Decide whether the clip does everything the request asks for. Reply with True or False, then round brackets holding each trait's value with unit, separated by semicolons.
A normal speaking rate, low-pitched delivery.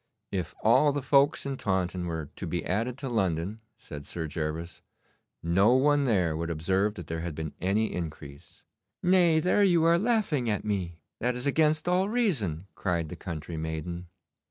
True (175 wpm; 100 Hz)